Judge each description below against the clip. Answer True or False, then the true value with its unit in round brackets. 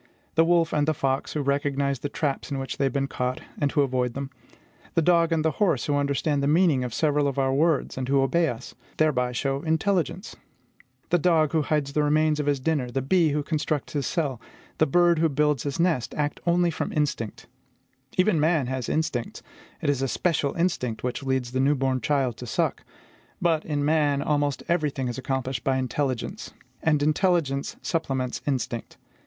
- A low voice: False (145 Hz)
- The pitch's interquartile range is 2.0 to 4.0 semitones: True (3.1 semitones)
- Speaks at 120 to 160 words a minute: False (195 wpm)